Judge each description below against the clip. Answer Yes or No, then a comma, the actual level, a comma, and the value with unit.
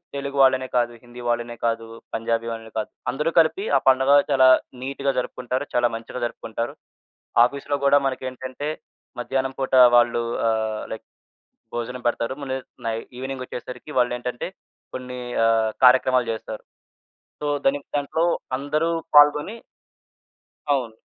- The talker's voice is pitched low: Yes, low, 130 Hz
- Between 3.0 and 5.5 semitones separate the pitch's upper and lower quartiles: No, narrow, 2.6 semitones